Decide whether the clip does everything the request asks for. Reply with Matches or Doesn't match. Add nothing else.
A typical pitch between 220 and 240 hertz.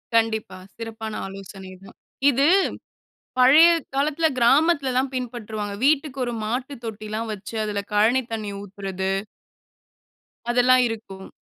Matches